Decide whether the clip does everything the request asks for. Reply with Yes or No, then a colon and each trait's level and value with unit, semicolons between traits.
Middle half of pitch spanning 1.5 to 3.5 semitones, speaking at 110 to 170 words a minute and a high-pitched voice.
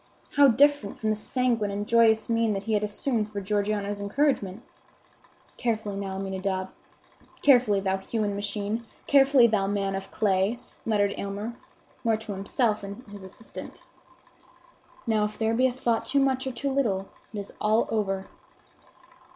Yes: average, 2.8 semitones; average, 155 wpm; high, 210 Hz